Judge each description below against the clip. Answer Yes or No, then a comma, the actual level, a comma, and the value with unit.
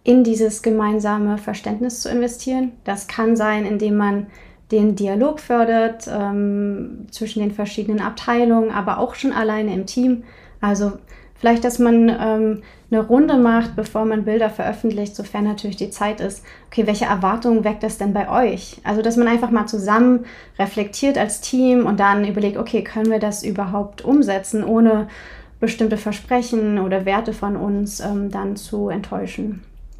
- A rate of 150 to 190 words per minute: Yes, average, 160 wpm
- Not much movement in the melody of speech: Yes, narrow, 2.1 semitones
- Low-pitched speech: No, high, 215 Hz